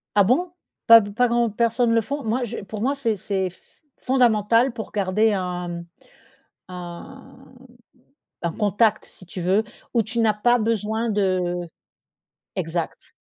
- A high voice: Yes, high, 215 Hz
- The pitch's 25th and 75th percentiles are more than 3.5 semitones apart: Yes, average, 3.9 semitones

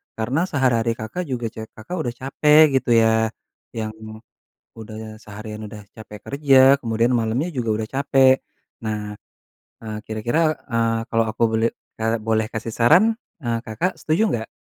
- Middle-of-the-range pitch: No, low, 115 Hz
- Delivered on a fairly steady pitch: No, average, 3.1 semitones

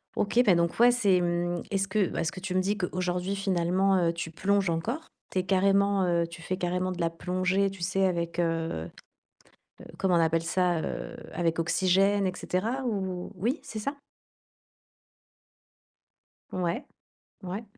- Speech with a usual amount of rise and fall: No, narrow, 2.3 semitones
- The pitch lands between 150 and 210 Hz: Yes, medium, 185 Hz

